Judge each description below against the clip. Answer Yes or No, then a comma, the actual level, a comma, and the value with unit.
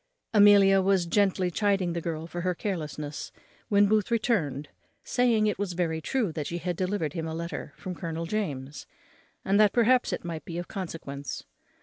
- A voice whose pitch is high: No, medium, 180 Hz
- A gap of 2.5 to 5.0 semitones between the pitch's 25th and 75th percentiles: Yes, average, 4.0 semitones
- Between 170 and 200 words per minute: Yes, average, 180 wpm